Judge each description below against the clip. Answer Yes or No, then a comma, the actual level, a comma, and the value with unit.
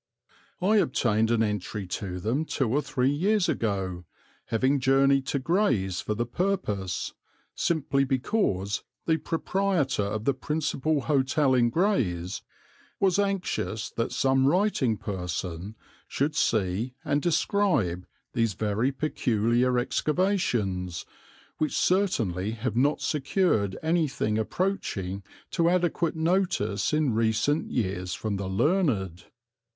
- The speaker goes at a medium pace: No, slow, 115 wpm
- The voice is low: Yes, low, 130 Hz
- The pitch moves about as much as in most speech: No, wide, 7.5 semitones